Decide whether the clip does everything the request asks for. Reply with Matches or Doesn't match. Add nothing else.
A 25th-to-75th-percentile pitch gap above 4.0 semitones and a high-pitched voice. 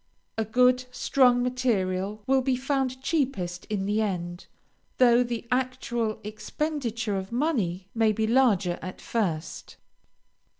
Matches